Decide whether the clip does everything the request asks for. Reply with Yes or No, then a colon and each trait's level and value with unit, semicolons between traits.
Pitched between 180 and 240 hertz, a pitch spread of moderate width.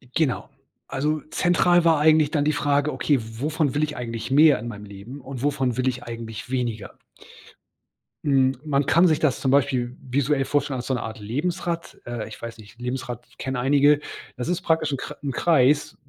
No: low, 135 Hz; average, 3.7 semitones